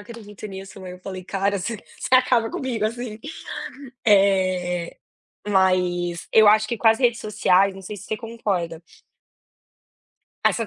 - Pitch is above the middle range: Yes, high, 200 Hz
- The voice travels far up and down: No, average, 3.2 semitones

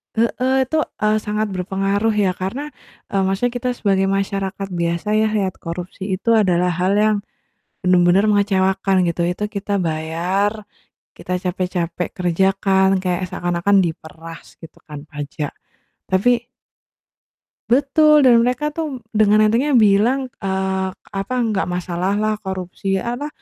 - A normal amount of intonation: Yes, average, 3.0 semitones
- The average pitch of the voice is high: Yes, high, 195 Hz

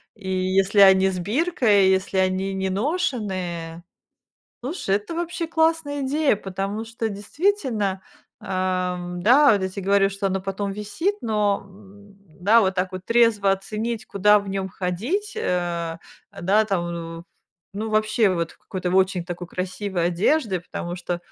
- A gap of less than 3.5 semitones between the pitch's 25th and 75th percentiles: Yes, average, 3.1 semitones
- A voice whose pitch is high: Yes, high, 195 Hz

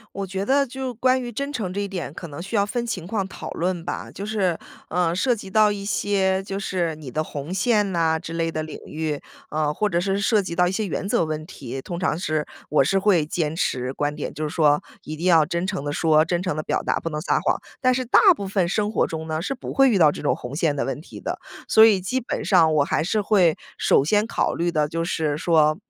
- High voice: No, medium, 175 Hz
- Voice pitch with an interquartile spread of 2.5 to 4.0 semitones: No, average, 4.5 semitones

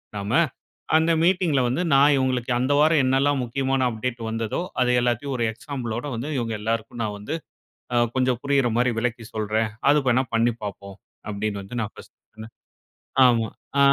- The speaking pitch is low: Yes, low, 120 Hz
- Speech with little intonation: No, average, 3.3 semitones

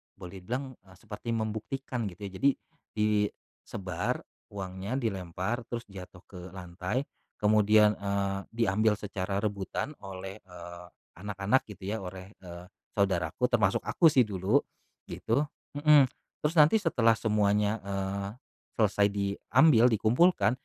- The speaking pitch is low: Yes, low, 105 Hz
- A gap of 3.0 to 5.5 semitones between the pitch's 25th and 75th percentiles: Yes, average, 3.4 semitones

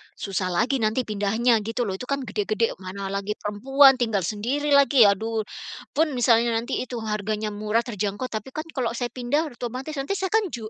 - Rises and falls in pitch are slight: No, average, 3.8 semitones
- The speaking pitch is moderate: No, high, 230 Hz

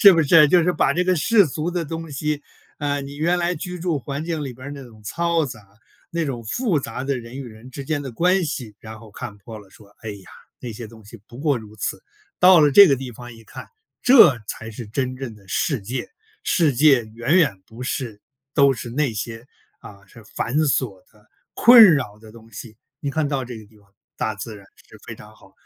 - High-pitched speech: No, low, 130 Hz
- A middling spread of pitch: No, wide, 5.8 semitones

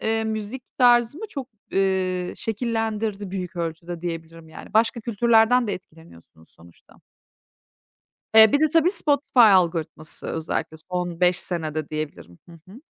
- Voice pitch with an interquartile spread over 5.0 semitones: Yes, wide, 5.4 semitones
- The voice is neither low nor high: No, high, 195 Hz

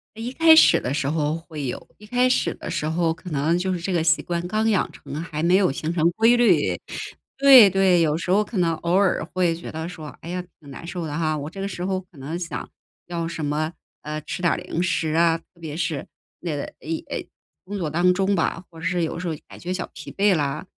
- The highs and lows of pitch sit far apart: No, average, 2.8 semitones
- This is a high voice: No, medium, 170 Hz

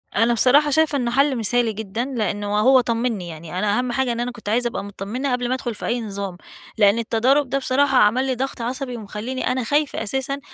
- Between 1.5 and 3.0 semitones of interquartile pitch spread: No, average, 3.7 semitones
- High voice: Yes, high, 240 Hz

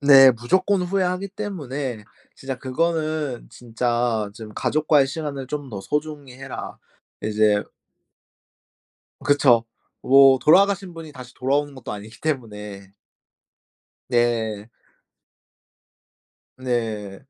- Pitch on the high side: No, low, 135 Hz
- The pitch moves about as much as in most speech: Yes, average, 4.9 semitones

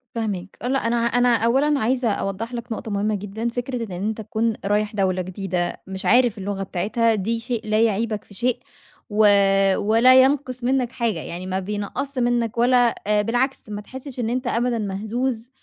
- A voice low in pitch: No, high, 230 Hz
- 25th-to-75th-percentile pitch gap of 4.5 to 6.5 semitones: No, average, 3.1 semitones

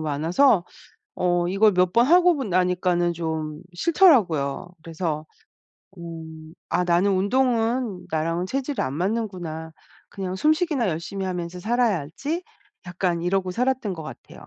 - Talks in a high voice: No, medium, 180 Hz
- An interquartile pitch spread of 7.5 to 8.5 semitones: No, wide, 5.6 semitones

